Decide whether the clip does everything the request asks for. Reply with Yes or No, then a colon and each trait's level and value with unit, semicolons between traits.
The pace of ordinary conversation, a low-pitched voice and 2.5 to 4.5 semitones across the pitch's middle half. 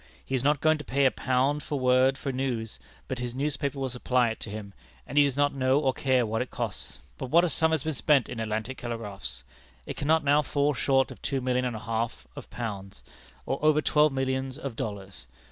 No: fast, 230 wpm; low, 130 Hz; average, 3.4 semitones